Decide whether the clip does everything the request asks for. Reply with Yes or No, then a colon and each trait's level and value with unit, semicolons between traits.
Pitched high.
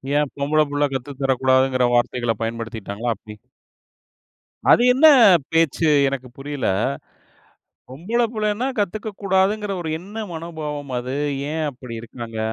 No: medium, 145 Hz